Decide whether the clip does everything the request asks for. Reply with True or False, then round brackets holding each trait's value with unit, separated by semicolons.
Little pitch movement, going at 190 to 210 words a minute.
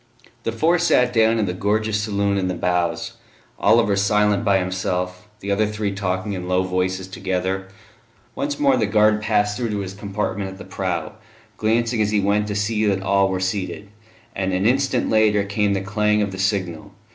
True (2.1 semitones; 195 wpm)